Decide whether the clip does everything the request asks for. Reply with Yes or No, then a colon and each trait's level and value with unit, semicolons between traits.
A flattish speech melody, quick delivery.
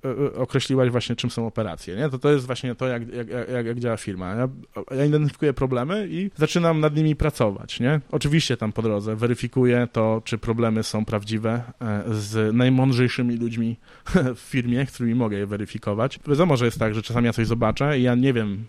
No: average, 3.0 semitones; fast, 195 wpm